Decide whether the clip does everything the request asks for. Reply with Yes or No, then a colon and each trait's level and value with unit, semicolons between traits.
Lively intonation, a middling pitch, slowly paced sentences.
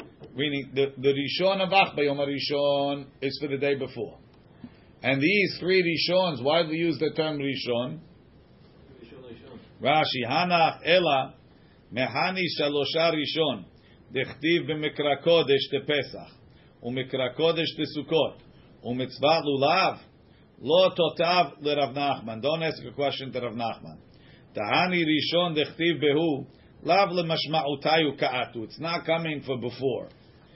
No: average, 3.1 semitones; medium, 145 Hz; slow, 120 wpm